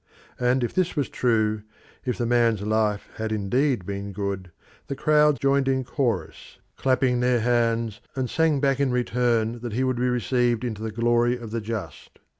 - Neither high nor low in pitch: No, low, 120 Hz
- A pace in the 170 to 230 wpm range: Yes, average, 180 wpm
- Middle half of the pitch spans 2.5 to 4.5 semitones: Yes, average, 2.9 semitones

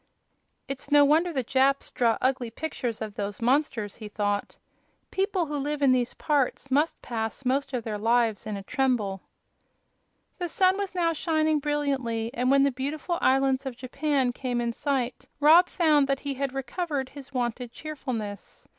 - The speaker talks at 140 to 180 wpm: Yes, average, 170 wpm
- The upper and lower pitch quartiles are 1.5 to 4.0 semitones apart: Yes, average, 3.6 semitones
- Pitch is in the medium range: No, very high, 270 Hz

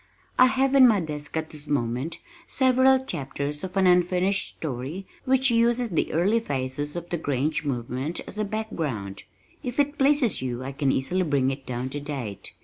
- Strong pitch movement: Yes, wide, 9.0 semitones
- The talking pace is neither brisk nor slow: Yes, average, 180 wpm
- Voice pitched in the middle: Yes, medium, 160 Hz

